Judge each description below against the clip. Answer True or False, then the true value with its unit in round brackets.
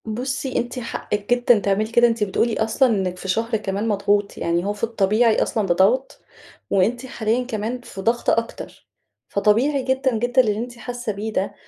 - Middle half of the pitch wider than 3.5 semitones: False (3.1 semitones)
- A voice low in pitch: False (225 Hz)